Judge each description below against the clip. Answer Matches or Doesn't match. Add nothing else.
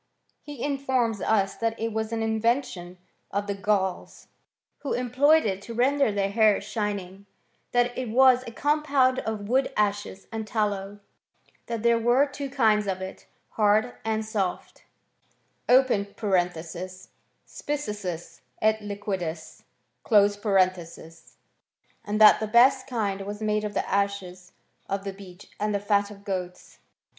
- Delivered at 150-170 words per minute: Doesn't match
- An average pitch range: Matches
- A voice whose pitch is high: Matches